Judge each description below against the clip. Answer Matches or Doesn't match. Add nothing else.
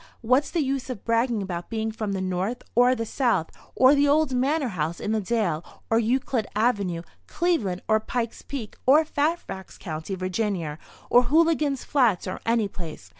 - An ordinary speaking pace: Matches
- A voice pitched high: Matches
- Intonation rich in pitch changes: Matches